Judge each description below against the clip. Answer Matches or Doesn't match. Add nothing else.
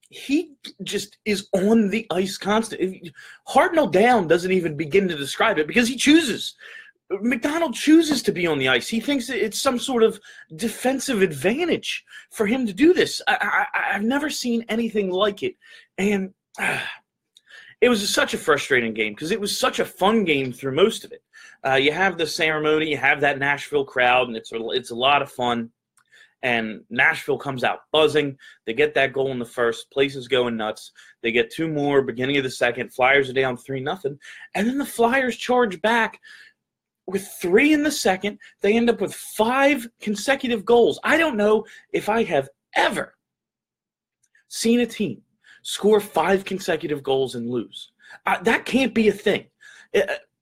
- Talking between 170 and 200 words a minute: Matches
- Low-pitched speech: Doesn't match